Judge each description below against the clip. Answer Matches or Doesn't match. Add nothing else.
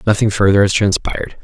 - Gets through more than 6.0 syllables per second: Matches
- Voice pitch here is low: Matches